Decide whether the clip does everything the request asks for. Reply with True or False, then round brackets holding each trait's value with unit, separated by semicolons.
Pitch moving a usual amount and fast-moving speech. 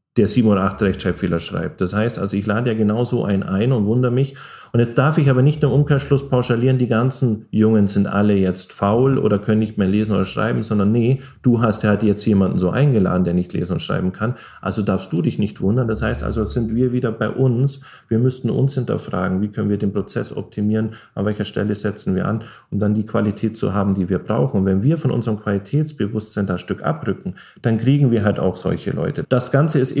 True (3.7 semitones; 235 wpm)